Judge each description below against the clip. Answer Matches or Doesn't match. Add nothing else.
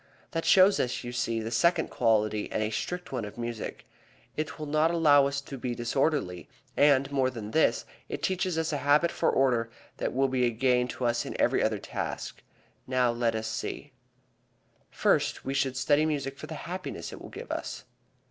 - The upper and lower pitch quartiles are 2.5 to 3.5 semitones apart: Doesn't match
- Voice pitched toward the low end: Matches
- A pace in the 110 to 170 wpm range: Doesn't match